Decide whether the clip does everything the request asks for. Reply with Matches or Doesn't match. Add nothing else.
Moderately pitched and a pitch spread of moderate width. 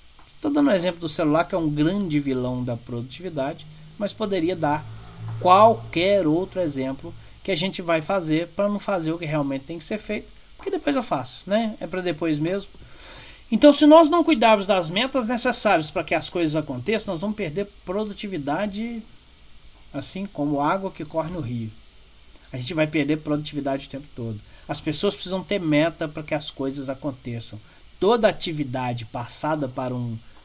Doesn't match